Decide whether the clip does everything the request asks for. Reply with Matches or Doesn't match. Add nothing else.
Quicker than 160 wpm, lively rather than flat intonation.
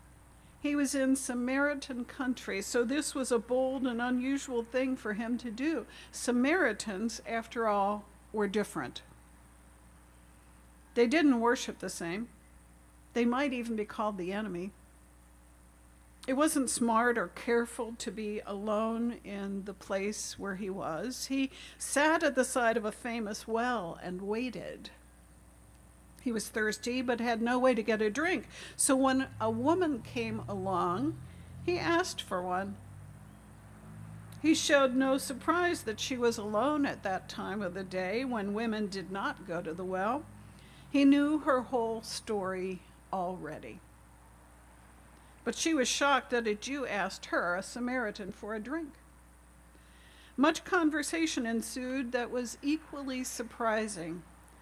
Doesn't match